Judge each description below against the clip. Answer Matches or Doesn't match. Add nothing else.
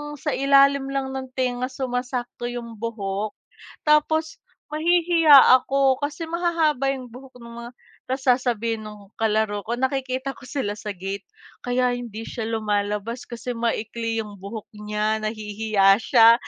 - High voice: Matches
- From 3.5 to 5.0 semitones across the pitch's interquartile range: Matches